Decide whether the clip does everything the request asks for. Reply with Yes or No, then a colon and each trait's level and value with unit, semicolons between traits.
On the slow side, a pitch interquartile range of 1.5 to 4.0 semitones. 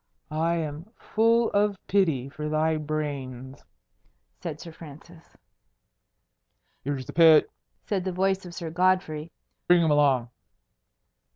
Yes: slow, 120 wpm; average, 3.6 semitones